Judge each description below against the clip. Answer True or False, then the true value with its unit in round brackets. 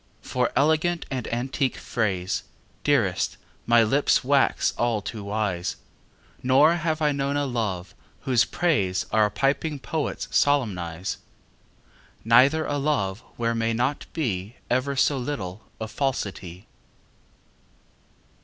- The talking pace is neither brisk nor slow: False (115 wpm)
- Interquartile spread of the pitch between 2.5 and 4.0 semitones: False (5.4 semitones)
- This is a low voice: True (125 Hz)